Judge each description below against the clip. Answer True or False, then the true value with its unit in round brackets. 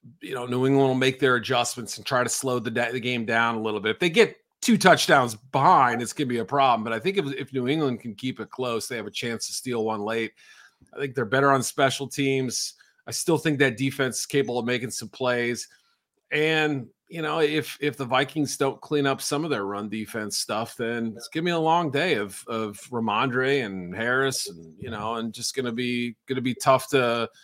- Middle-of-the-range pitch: False (130 Hz)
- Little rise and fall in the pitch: False (3.2 semitones)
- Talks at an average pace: False (245 wpm)